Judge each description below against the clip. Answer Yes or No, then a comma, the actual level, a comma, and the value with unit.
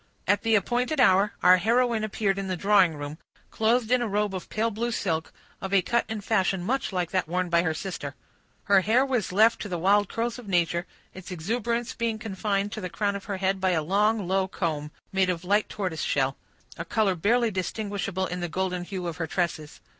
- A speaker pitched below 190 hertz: No, high, 195 Hz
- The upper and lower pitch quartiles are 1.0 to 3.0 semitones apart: No, average, 3.4 semitones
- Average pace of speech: No, fast, 215 wpm